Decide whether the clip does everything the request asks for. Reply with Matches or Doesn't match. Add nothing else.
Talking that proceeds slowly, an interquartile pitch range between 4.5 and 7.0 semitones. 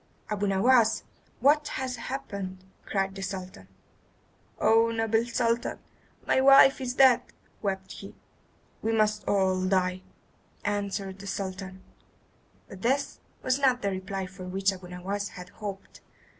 Doesn't match